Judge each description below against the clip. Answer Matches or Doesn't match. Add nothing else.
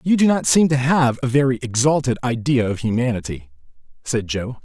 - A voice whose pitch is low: Matches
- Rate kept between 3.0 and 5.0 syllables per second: Doesn't match